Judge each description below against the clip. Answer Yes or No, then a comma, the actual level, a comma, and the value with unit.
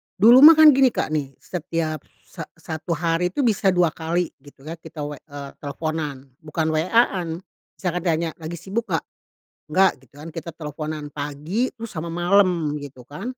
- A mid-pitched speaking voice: Yes, medium, 165 Hz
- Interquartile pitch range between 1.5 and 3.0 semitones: No, average, 3.6 semitones